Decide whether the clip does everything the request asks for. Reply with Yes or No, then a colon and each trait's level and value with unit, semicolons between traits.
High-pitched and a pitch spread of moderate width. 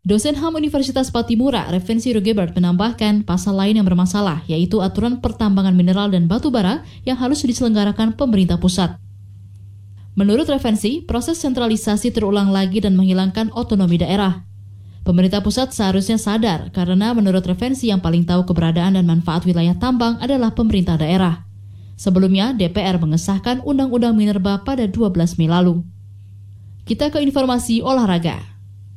Yes: high, 200 Hz; average, 4.9 semitones